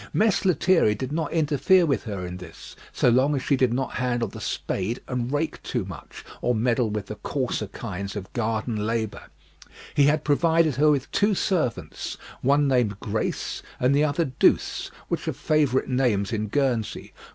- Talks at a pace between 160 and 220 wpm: Yes, average, 175 wpm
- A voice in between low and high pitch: No, low, 130 Hz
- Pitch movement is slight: No, average, 5.0 semitones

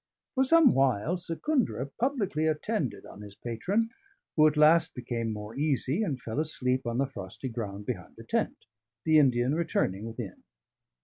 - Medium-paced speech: Yes, average, 160 wpm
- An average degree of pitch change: No, wide, 6.1 semitones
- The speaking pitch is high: No, low, 135 Hz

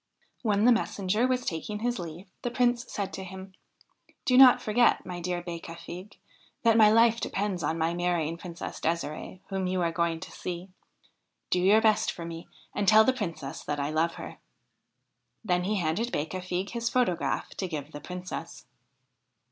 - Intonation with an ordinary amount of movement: Yes, average, 4.4 semitones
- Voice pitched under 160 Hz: No, medium, 185 Hz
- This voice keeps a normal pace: Yes, average, 175 wpm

